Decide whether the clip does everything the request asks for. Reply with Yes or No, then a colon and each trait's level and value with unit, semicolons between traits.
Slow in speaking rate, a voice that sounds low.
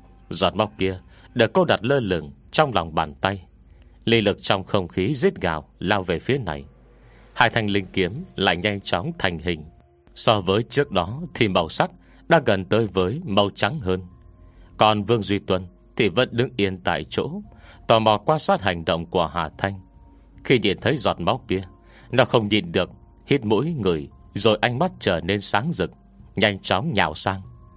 No: average, 190 wpm; very low, 95 Hz